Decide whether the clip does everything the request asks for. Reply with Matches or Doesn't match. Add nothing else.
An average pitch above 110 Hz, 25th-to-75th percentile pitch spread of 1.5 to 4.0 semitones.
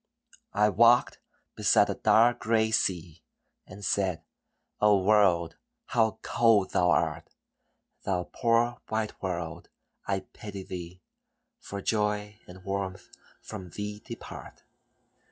Doesn't match